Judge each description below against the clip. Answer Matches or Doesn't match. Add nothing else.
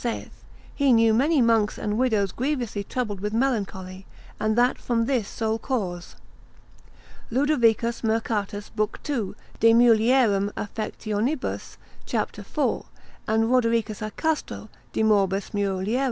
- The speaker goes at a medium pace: Doesn't match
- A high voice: Matches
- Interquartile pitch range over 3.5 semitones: Doesn't match